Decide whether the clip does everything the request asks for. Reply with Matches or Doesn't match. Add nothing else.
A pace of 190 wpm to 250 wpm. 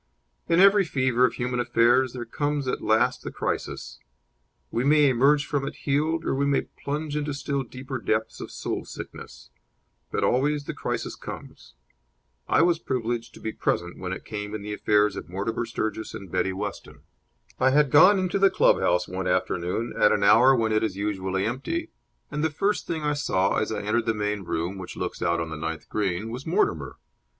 Matches